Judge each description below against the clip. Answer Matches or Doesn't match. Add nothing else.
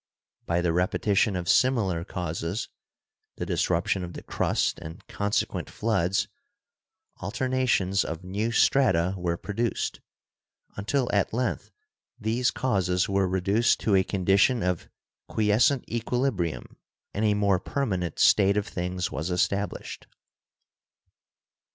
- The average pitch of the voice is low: Matches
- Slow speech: Matches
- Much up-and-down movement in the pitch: Doesn't match